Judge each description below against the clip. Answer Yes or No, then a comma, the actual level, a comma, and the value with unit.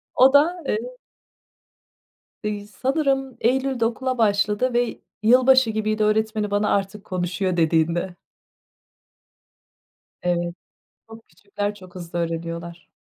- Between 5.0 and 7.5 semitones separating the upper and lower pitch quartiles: Yes, wide, 5.6 semitones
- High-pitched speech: Yes, high, 210 Hz